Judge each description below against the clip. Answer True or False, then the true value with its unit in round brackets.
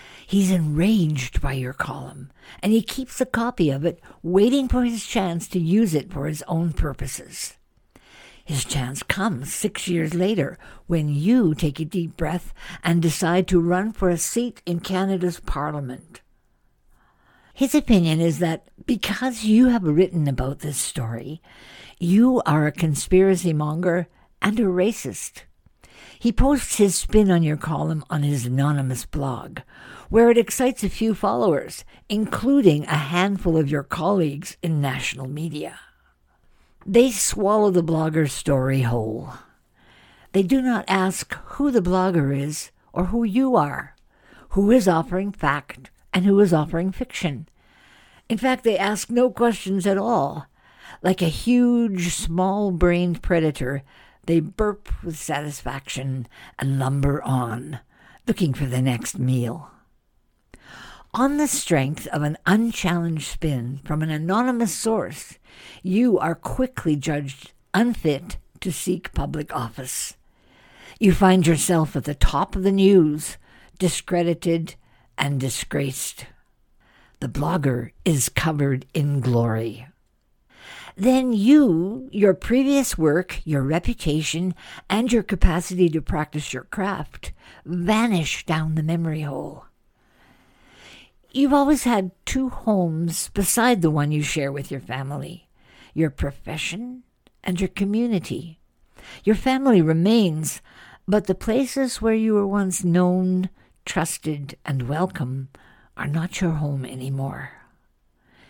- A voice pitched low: False (175 Hz)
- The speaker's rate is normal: False (130 wpm)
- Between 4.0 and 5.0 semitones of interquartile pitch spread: False (5.6 semitones)